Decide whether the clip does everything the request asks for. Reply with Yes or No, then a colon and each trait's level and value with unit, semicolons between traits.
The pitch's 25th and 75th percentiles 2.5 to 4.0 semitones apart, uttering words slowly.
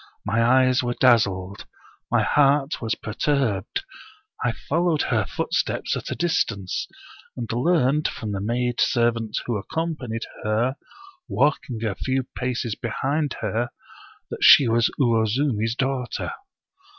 Yes: average, 3.4 semitones; slow, 125 wpm